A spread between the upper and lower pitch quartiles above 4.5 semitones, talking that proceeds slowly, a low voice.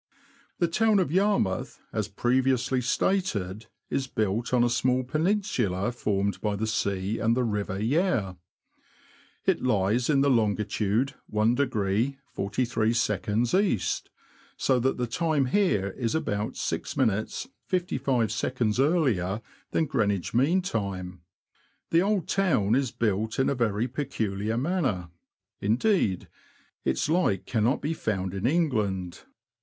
Yes: average, 5.3 semitones; slow, 125 wpm; low, 120 Hz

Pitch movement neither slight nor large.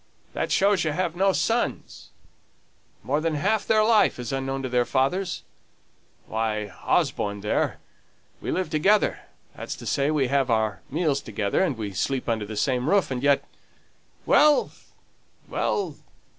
No: wide, 7.8 semitones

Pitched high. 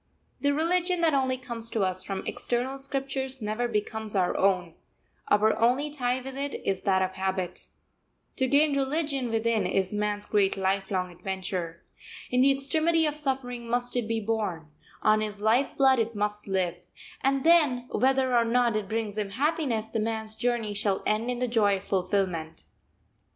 Yes: high, 230 Hz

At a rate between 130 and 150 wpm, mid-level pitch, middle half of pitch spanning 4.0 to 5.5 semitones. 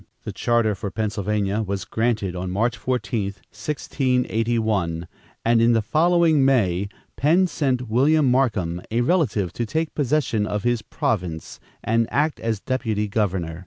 No: average, 140 wpm; low, 115 Hz; average, 4.5 semitones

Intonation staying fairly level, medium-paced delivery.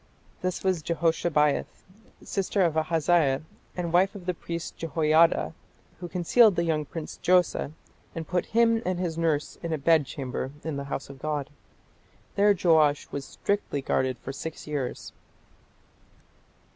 No: average, 3.2 semitones; average, 145 wpm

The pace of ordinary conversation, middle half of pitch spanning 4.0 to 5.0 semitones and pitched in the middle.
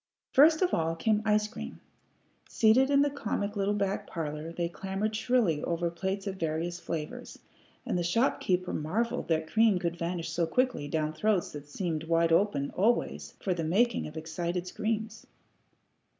Yes: average, 165 wpm; average, 4.7 semitones; medium, 180 Hz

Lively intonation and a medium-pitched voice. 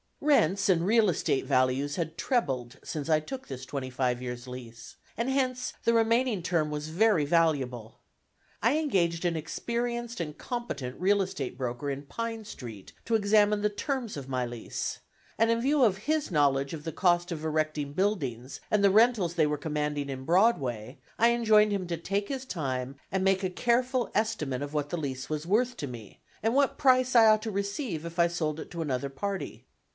Yes: wide, 7.9 semitones; medium, 170 Hz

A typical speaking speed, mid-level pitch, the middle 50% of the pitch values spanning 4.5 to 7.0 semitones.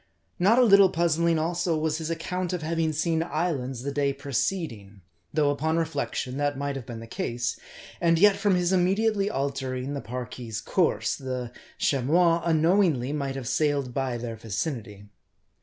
Yes: average, 160 wpm; medium, 150 Hz; average, 4.9 semitones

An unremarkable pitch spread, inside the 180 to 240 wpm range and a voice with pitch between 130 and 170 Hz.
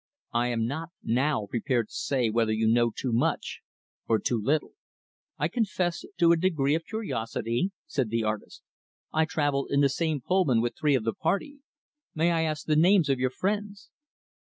No: wide, 6.1 semitones; average, 185 wpm; medium, 140 Hz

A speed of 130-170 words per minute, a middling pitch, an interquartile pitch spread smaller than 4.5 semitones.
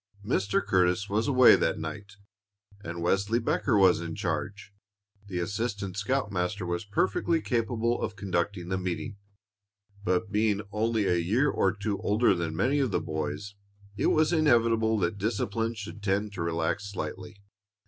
No: average, 150 wpm; low, 100 Hz; average, 3.4 semitones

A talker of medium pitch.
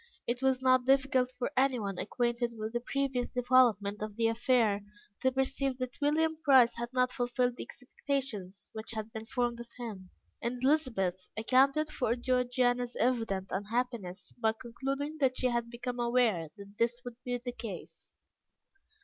No: high, 245 Hz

